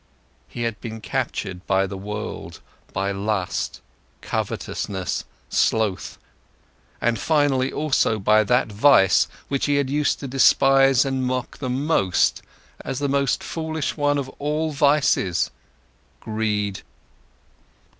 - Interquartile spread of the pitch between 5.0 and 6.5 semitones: Yes, wide, 5.4 semitones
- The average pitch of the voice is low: Yes, low, 125 Hz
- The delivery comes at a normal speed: No, slow, 120 wpm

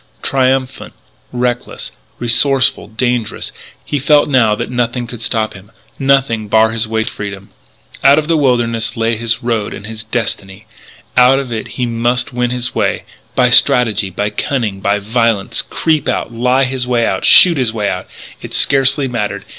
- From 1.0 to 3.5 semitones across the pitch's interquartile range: Yes, average, 2.7 semitones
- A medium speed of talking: Yes, average, 170 wpm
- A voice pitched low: Yes, low, 120 Hz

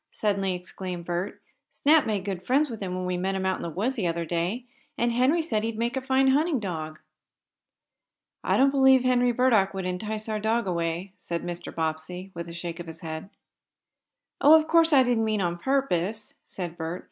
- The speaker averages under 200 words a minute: No, fast, 205 wpm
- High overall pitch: Yes, high, 195 Hz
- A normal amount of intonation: No, wide, 6.2 semitones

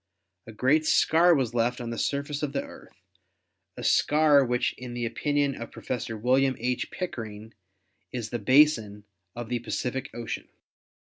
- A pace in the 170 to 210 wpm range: No, average, 155 wpm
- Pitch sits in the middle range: No, low, 125 Hz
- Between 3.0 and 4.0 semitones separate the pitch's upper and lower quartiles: Yes, average, 3.4 semitones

